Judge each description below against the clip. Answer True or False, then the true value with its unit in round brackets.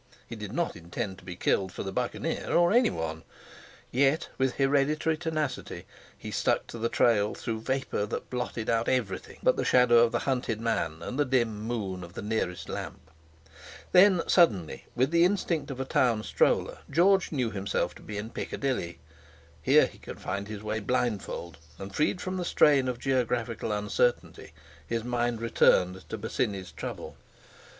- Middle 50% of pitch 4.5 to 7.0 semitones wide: True (4.9 semitones)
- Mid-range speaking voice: False (115 Hz)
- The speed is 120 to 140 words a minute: False (170 wpm)